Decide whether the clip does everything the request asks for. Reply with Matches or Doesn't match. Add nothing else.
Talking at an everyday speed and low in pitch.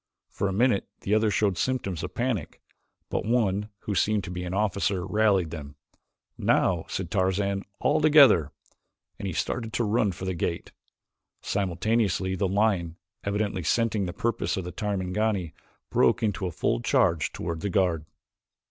Matches